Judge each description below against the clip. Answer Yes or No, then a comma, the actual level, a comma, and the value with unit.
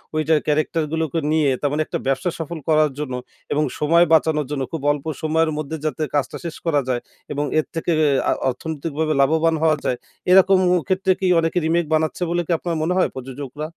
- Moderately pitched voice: Yes, medium, 155 Hz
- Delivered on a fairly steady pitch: Yes, narrow, 1.9 semitones